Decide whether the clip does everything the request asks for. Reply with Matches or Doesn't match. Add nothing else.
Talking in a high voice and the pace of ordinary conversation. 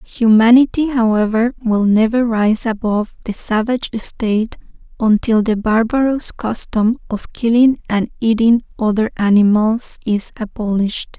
Doesn't match